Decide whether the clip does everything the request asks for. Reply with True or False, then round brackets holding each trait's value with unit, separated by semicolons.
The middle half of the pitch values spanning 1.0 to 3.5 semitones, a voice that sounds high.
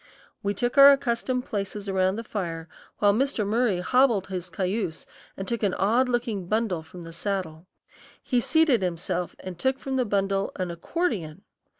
False (4.9 semitones; 200 Hz)